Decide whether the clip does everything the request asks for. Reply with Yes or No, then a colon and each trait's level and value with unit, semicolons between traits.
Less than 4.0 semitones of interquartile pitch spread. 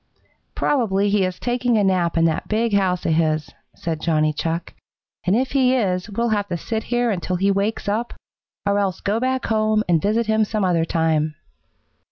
No: average, 4.4 semitones